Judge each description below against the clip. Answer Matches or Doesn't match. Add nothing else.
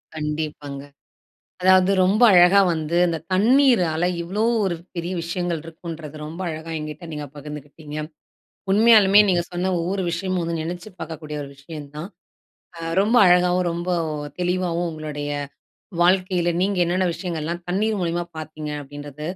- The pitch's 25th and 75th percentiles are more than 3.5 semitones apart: Doesn't match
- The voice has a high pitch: Doesn't match